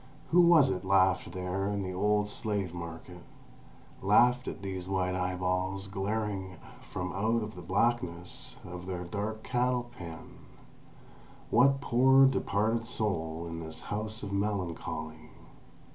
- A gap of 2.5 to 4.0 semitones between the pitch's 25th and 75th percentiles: Yes, average, 3.2 semitones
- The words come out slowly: Yes, slow, 130 wpm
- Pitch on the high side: No, very low, 95 Hz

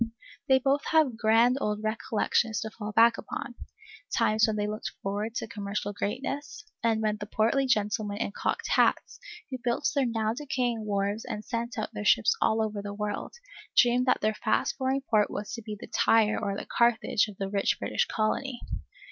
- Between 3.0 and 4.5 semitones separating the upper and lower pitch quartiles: No, narrow, 2.6 semitones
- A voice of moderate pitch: No, high, 220 Hz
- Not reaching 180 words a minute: No, average, 190 wpm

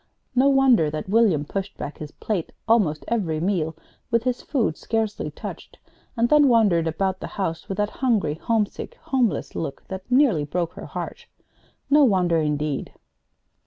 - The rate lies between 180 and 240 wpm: No, average, 160 wpm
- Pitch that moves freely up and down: Yes, wide, 6.4 semitones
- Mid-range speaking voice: No, high, 195 Hz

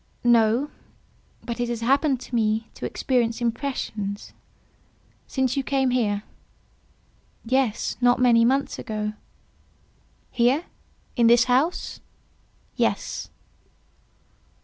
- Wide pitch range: No, narrow, 2.5 semitones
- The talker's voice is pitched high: Yes, high, 240 Hz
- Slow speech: Yes, slow, 95 wpm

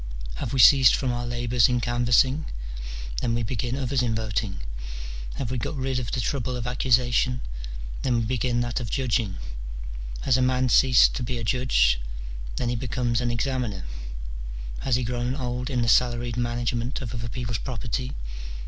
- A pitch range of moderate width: No, narrow, 1.5 semitones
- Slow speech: No, average, 175 wpm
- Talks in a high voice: No, low, 120 Hz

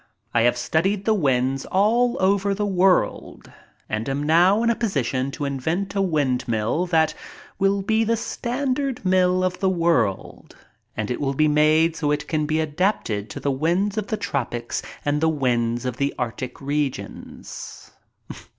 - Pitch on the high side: No, medium, 160 Hz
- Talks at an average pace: Yes, average, 165 wpm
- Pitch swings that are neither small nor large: No, wide, 6.5 semitones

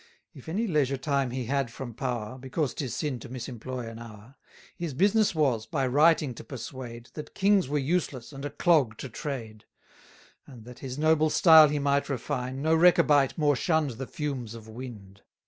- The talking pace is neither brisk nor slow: Yes, average, 180 wpm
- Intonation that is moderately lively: Yes, average, 3.9 semitones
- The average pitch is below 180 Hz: Yes, low, 135 Hz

